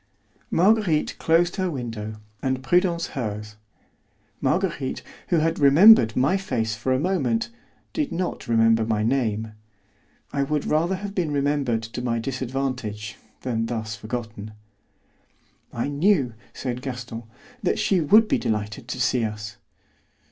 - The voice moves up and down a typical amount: No, wide, 6.9 semitones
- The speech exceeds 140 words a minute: No, slow, 135 wpm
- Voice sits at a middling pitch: No, low, 130 Hz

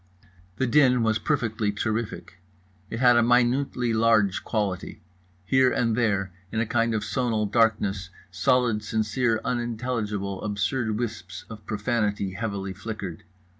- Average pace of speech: No, slow, 130 wpm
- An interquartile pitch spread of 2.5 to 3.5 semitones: Yes, average, 2.8 semitones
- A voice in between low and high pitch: No, low, 110 Hz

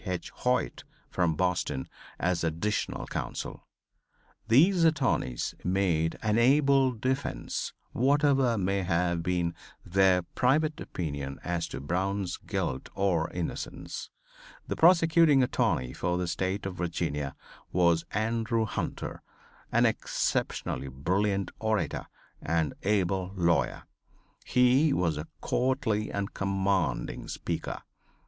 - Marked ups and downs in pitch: Yes, wide, 6.0 semitones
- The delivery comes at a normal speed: No, slow, 105 wpm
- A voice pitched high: No, very low, 95 Hz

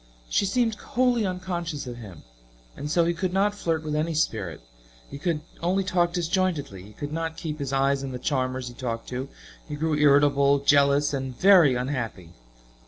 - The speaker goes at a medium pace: Yes, average, 180 wpm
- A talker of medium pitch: Yes, medium, 145 Hz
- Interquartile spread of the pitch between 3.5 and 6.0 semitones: Yes, average, 4.7 semitones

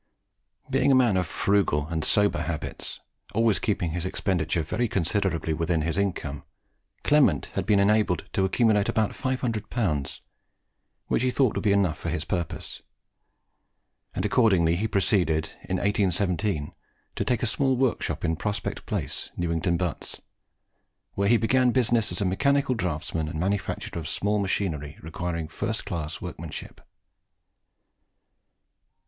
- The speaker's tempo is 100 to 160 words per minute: Yes, average, 140 wpm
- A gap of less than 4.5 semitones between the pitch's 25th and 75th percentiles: No, average, 5.0 semitones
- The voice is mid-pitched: No, very low, 95 Hz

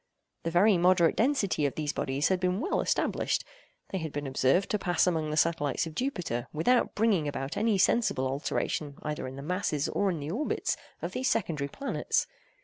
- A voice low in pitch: No, medium, 165 Hz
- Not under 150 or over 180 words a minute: No, average, 190 wpm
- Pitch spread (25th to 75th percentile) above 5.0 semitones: Yes, wide, 5.4 semitones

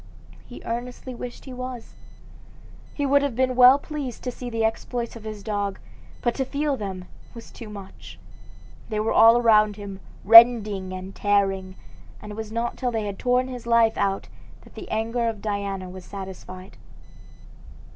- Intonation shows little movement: No, average, 3.6 semitones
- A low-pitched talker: No, high, 225 Hz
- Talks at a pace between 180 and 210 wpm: No, average, 170 wpm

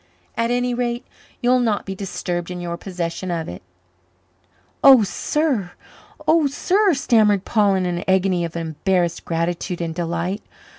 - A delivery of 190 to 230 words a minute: No, average, 145 wpm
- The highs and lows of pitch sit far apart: Yes, wide, 5.7 semitones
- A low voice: No, high, 190 Hz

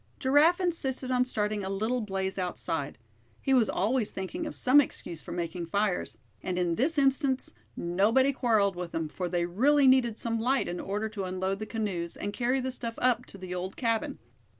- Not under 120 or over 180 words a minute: No, average, 195 wpm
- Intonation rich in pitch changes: Yes, wide, 5.8 semitones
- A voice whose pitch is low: No, high, 215 Hz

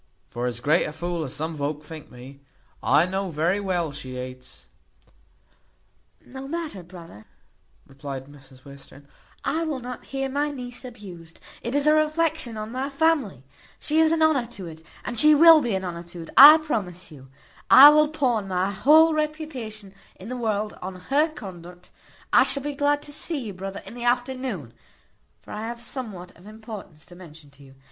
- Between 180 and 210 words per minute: Yes, average, 185 wpm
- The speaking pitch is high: Yes, high, 210 Hz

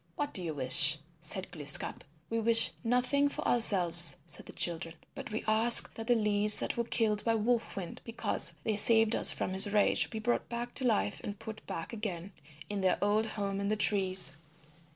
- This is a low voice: No, high, 210 Hz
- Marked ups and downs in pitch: No, average, 3.4 semitones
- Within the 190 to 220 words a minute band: Yes, average, 195 wpm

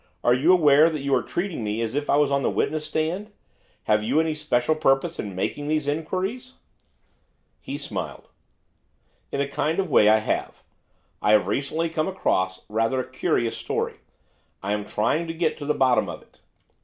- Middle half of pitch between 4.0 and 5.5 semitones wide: Yes, average, 5.0 semitones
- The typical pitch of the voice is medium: Yes, medium, 145 Hz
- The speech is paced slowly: No, average, 190 wpm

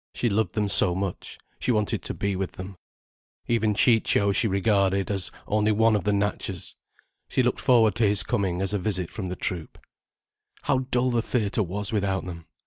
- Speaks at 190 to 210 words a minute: Yes, average, 195 wpm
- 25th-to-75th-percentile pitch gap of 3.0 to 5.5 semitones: No, narrow, 2.6 semitones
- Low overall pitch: Yes, low, 100 Hz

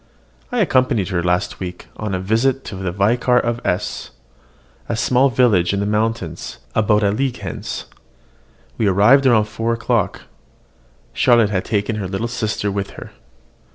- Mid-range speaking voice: No, low, 105 Hz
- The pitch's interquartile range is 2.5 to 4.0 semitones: Yes, average, 3.4 semitones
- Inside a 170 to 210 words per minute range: No, average, 155 wpm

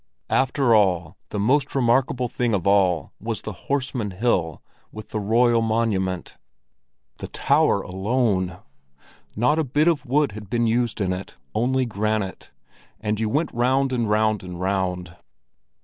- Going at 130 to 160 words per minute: Yes, average, 150 wpm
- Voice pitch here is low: Yes, low, 110 Hz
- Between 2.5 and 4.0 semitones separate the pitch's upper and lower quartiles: No, average, 4.5 semitones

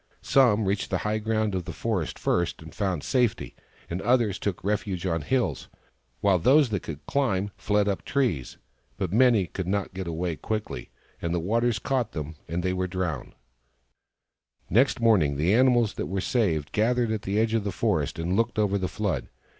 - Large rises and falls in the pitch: No, average, 4.2 semitones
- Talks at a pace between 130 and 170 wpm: No, average, 185 wpm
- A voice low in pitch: Yes, low, 100 Hz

